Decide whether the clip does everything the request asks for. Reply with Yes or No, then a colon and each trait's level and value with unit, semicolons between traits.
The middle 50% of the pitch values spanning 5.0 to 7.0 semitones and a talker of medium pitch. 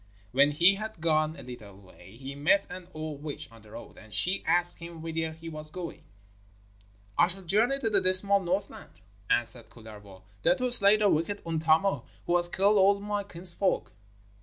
Yes: wide, 5.4 semitones; medium, 170 Hz